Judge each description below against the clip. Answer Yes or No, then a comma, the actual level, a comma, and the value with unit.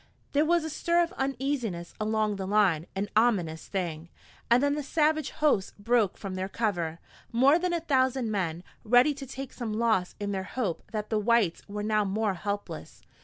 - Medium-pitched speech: No, high, 215 Hz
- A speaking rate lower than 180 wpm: No, average, 185 wpm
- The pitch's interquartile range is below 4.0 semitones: No, wide, 5.6 semitones